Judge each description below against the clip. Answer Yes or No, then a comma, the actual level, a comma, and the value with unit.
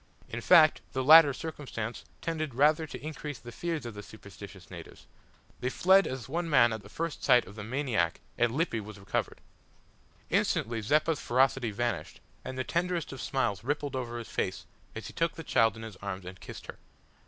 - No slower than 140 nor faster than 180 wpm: No, average, 190 wpm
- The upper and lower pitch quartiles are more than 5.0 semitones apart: Yes, wide, 5.4 semitones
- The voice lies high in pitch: No, low, 130 Hz